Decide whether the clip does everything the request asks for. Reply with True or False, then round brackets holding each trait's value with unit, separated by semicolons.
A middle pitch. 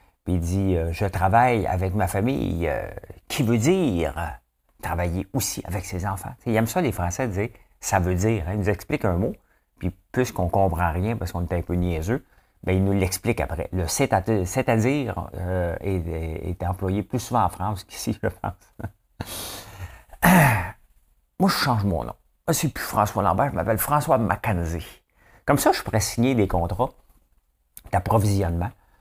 False (95 Hz)